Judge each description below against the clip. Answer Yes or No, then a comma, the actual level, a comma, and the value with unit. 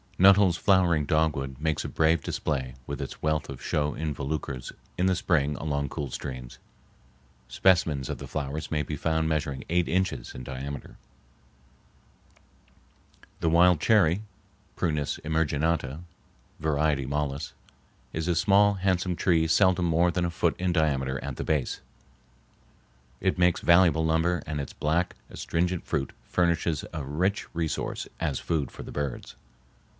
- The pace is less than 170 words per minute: Yes, average, 140 wpm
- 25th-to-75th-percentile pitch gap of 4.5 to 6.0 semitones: No, average, 3.5 semitones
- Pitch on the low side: Yes, very low, 80 Hz